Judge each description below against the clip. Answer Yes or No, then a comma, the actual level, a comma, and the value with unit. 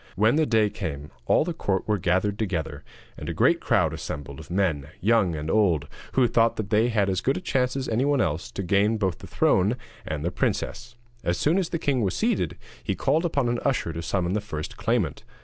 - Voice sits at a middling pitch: No, low, 105 Hz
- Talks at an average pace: No, fast, 220 wpm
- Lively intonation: Yes, wide, 5.8 semitones